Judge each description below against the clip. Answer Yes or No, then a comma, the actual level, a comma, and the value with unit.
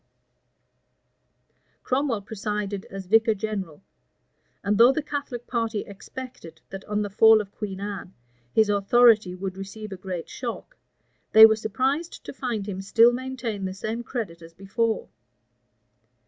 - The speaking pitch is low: No, high, 215 Hz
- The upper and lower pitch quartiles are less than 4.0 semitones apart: Yes, average, 3.3 semitones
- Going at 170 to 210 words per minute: No, average, 140 wpm